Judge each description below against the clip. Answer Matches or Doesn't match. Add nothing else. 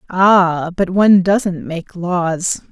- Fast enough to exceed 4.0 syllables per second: Doesn't match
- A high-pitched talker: Doesn't match